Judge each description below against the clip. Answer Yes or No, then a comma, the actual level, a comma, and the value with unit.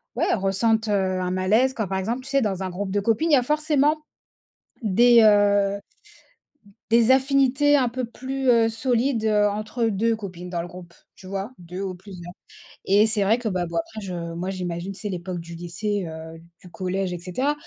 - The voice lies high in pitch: Yes, high, 205 Hz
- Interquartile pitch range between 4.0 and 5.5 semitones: Yes, average, 4.3 semitones